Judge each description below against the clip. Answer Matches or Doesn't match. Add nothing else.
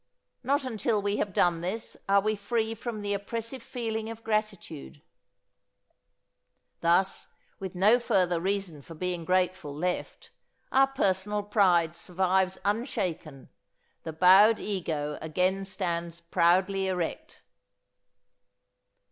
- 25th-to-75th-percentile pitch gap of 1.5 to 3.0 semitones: Doesn't match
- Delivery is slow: Matches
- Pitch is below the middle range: Doesn't match